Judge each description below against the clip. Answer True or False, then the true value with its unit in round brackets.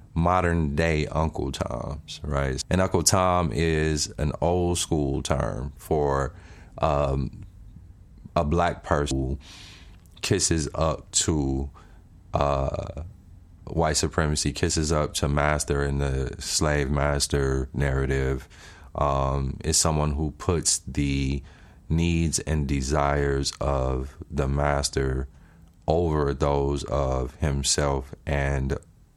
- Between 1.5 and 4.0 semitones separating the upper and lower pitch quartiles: True (3.5 semitones)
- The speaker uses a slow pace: True (105 wpm)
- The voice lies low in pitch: True (75 Hz)